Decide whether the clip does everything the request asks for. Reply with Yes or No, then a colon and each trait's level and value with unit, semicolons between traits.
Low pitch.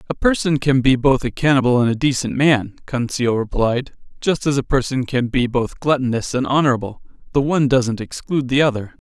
Yes: low, 130 Hz